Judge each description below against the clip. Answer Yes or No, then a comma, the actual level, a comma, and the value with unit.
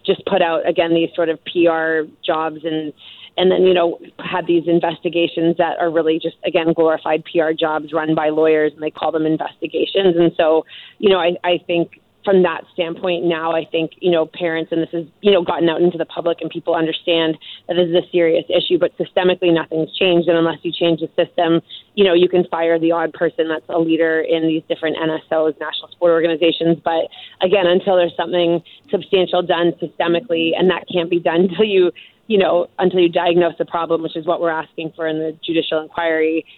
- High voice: No, medium, 170 Hz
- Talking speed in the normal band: No, fast, 210 wpm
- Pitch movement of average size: No, narrow, 1.5 semitones